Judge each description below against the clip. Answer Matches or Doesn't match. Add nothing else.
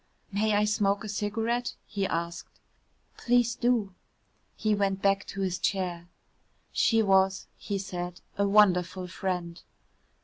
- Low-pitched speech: Doesn't match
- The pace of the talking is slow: Matches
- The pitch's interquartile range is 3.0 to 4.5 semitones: Doesn't match